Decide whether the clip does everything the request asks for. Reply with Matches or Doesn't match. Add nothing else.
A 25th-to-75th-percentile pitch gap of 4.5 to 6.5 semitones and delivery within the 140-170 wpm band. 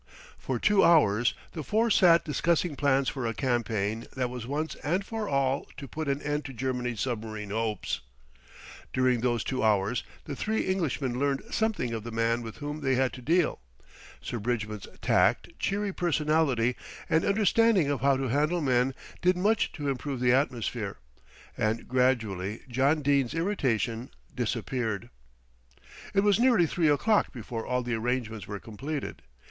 Matches